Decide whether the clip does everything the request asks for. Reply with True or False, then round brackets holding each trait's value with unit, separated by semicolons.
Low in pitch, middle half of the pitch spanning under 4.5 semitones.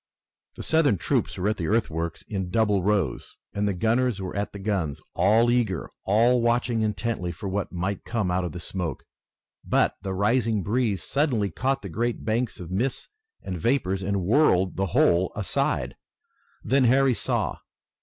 True (100 Hz; 4.1 semitones)